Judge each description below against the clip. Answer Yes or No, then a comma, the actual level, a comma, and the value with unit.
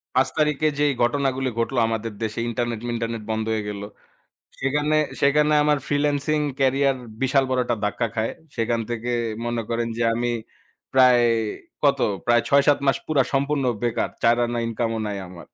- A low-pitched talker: Yes, low, 125 Hz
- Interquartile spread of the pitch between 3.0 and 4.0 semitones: Yes, average, 3.3 semitones